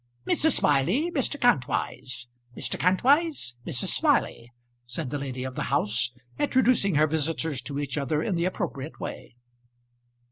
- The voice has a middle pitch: Yes, medium, 150 Hz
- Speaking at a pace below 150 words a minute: Yes, average, 140 wpm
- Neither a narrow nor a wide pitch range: No, wide, 7.3 semitones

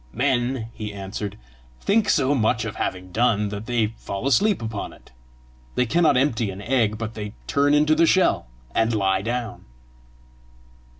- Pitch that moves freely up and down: No, average, 4.4 semitones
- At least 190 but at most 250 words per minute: No, average, 160 wpm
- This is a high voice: No, low, 115 Hz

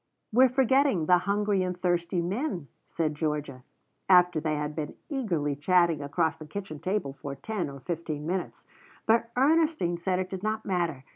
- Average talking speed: Yes, average, 165 wpm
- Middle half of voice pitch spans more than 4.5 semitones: Yes, average, 5.1 semitones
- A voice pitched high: No, medium, 175 Hz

